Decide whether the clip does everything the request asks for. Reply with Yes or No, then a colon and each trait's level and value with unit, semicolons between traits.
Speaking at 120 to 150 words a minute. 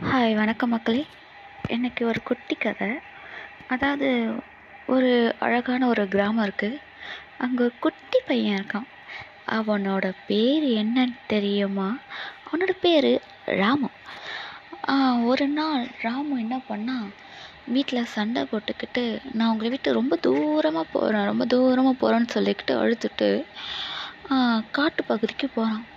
No: average, 105 wpm